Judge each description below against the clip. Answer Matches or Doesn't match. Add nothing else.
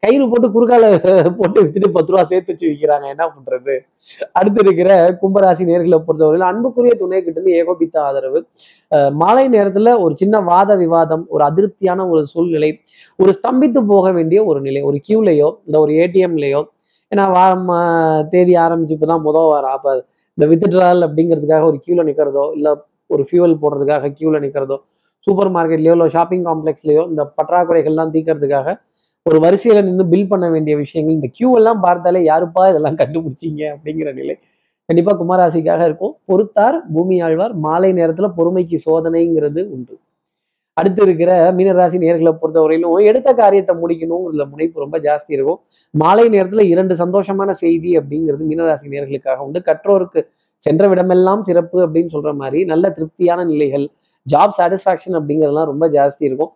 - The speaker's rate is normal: Doesn't match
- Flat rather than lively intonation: Doesn't match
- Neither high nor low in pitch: Matches